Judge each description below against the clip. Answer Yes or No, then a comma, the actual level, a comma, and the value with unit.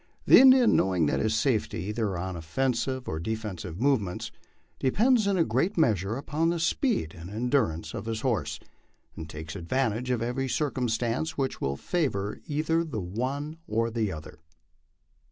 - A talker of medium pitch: No, low, 115 Hz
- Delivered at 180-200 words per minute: No, average, 155 wpm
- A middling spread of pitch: No, wide, 6.7 semitones